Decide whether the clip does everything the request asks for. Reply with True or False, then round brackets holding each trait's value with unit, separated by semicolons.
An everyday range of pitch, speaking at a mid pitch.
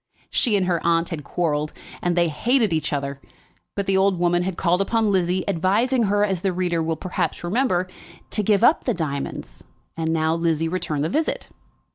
True (3.4 semitones; 175 Hz)